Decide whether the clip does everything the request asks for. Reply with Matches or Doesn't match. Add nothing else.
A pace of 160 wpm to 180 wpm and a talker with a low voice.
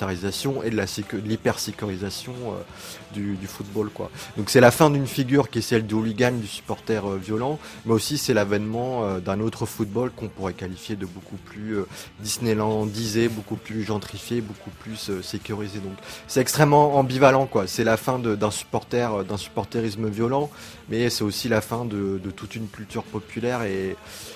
Doesn't match